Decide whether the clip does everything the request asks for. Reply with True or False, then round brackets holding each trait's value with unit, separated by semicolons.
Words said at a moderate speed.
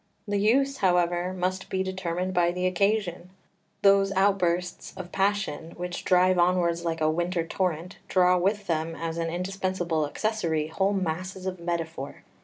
True (150 wpm)